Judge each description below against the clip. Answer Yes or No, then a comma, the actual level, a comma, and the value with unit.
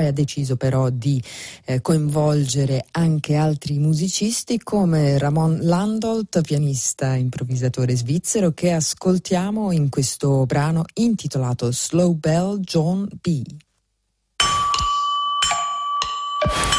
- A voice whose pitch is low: No, medium, 160 Hz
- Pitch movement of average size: No, wide, 6.1 semitones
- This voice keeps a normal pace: No, slow, 90 wpm